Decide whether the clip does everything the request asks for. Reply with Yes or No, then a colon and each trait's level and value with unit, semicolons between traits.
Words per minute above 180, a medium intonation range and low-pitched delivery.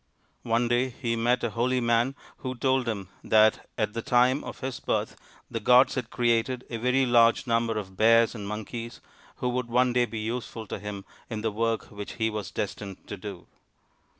No: average, 195 wpm; narrow, 2.3 semitones; low, 115 Hz